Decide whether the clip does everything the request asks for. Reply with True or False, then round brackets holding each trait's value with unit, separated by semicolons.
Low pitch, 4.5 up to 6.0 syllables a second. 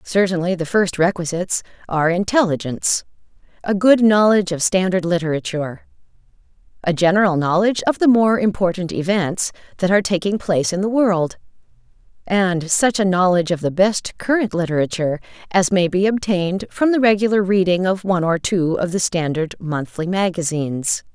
False (180 Hz; 5.6 syllables/s)